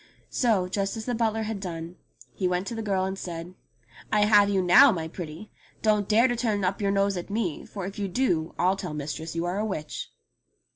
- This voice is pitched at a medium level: No, high, 195 Hz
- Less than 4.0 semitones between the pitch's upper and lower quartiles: Yes, average, 3.3 semitones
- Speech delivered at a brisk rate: Yes, fast, 225 wpm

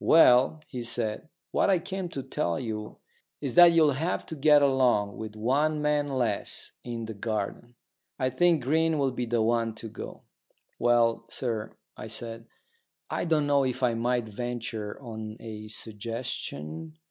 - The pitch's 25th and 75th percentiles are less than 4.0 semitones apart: No, average, 4.5 semitones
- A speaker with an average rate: Yes, average, 160 wpm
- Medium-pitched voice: No, low, 120 Hz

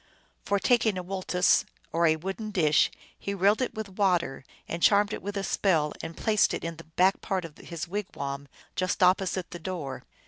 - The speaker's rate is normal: Yes, average, 195 wpm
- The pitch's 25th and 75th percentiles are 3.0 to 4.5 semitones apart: Yes, average, 3.3 semitones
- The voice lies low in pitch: No, medium, 185 Hz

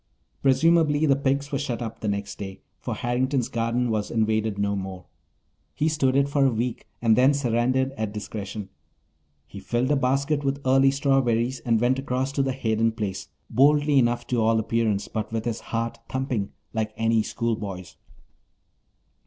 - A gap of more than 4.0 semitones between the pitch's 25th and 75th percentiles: No, average, 3.6 semitones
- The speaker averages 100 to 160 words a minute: No, average, 170 wpm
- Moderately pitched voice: No, low, 120 Hz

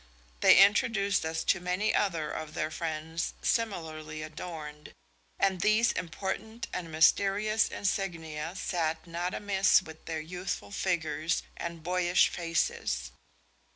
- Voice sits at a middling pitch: Yes, medium, 175 Hz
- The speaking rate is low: Yes, slow, 120 wpm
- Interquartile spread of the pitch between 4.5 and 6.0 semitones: No, average, 3.5 semitones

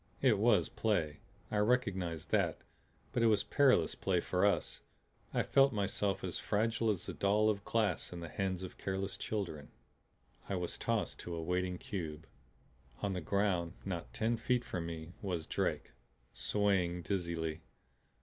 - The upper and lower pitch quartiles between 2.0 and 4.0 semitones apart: Yes, average, 3.6 semitones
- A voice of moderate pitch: No, very low, 95 Hz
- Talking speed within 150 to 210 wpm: Yes, average, 160 wpm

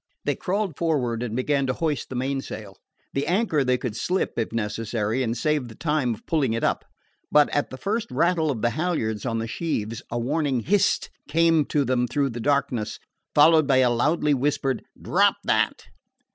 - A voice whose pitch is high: No, low, 135 Hz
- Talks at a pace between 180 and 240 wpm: Yes, average, 185 wpm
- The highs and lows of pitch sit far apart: No, average, 4.7 semitones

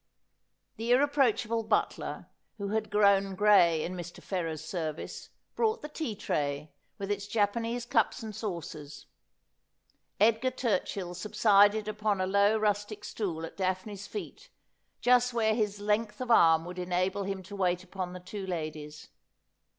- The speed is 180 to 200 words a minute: No, average, 145 wpm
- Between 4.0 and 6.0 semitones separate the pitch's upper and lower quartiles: No, average, 3.3 semitones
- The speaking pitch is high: Yes, high, 205 Hz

